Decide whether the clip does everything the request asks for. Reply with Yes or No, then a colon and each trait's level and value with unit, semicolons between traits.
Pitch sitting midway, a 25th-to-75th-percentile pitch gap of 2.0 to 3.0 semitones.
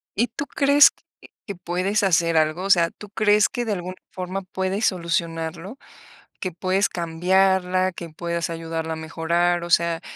Yes: medium, 180 Hz; narrow, 2.5 semitones